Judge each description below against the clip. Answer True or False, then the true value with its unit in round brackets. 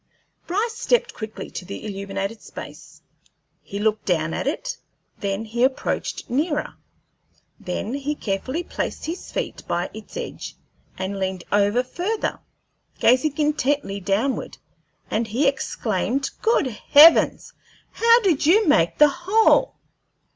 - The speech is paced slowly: True (125 wpm)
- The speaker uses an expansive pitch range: True (8.2 semitones)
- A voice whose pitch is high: True (255 Hz)